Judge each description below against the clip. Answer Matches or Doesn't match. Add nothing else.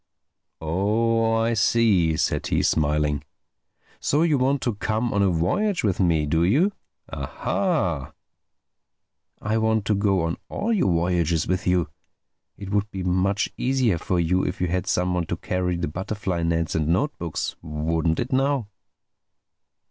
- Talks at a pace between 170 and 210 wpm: Doesn't match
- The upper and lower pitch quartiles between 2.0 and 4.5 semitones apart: Doesn't match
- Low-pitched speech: Matches